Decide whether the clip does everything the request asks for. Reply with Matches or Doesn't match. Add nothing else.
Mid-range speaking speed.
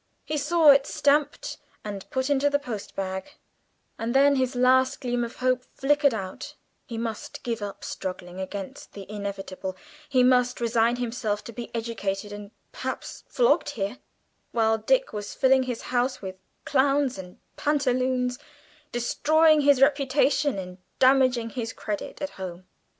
Matches